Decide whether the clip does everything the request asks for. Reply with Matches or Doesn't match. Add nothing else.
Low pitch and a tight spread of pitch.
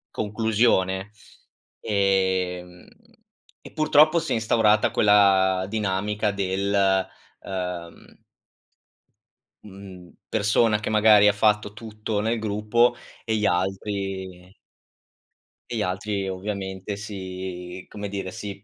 Matches